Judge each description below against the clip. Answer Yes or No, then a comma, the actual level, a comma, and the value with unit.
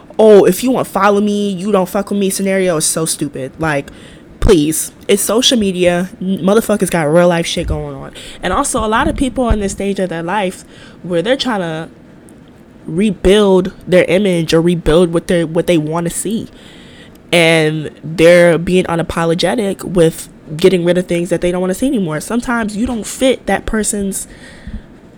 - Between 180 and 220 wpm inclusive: Yes, average, 185 wpm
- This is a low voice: No, medium, 185 Hz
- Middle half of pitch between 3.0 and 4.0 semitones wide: Yes, average, 3.4 semitones